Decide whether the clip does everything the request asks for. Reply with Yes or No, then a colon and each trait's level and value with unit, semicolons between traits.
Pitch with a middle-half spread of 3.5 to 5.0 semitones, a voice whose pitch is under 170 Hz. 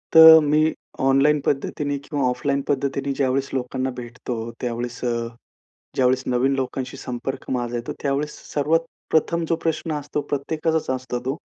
No: average, 2.9 semitones; low, 135 Hz